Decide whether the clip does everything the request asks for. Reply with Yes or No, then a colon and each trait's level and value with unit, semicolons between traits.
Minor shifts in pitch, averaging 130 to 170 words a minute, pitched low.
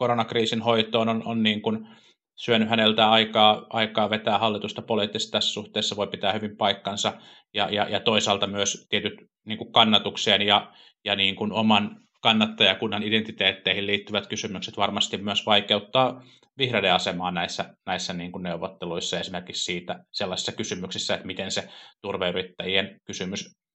Yes: narrow, 2.0 semitones; average, 140 wpm; low, 110 Hz